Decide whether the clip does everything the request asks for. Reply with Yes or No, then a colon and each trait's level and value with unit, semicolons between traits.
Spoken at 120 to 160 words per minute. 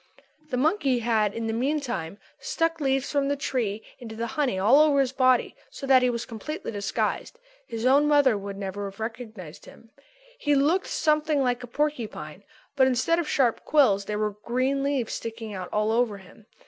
No: average, 185 wpm